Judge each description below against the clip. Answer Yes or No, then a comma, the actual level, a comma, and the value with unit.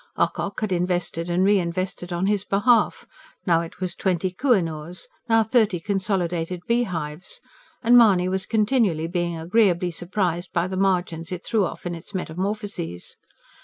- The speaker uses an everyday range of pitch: Yes, average, 3.0 semitones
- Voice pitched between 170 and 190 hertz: Yes, medium, 185 Hz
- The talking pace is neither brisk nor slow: Yes, average, 160 wpm